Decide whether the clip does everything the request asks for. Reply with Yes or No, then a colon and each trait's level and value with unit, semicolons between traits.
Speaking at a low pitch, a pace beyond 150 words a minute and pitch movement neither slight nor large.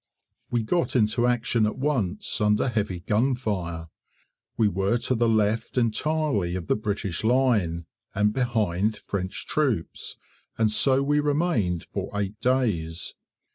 No: low, 110 Hz; slow, 135 wpm; average, 4.4 semitones